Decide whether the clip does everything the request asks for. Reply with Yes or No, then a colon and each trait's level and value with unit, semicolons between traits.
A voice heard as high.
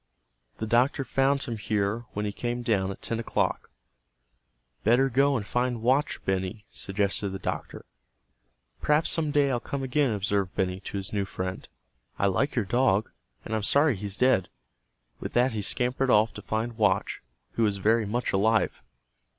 No: low, 110 Hz